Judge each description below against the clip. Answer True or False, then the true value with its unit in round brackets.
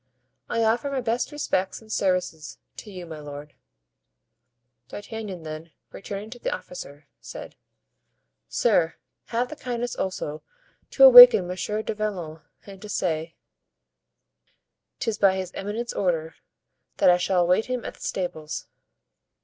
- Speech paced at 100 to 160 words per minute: True (140 wpm)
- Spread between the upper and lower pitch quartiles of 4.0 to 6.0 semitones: True (5.2 semitones)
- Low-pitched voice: False (190 Hz)